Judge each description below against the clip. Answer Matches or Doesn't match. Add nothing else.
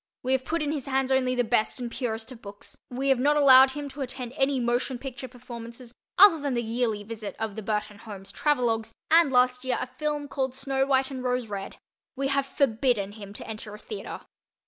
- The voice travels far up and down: Doesn't match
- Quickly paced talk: Matches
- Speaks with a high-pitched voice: Matches